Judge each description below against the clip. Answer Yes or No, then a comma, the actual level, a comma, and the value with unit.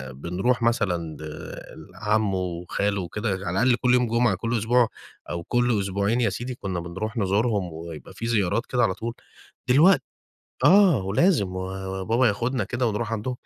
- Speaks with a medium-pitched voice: No, low, 105 Hz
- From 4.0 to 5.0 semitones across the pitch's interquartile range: Yes, average, 4.3 semitones